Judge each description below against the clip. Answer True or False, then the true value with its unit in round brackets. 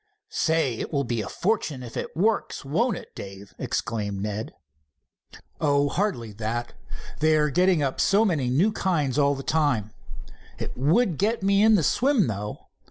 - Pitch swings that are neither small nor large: False (8.2 semitones)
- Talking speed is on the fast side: False (170 wpm)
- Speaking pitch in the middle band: True (145 Hz)